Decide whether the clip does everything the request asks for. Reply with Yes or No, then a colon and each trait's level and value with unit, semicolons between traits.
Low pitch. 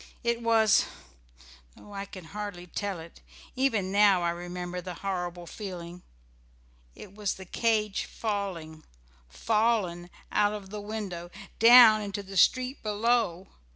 No: high, 200 Hz